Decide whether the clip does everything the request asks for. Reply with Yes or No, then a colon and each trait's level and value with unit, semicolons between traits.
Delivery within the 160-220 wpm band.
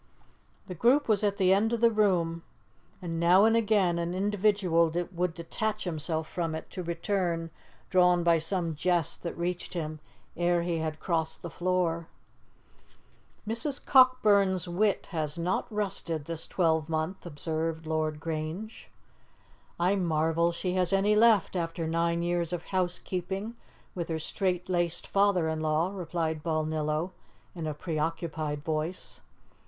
No: average, 140 wpm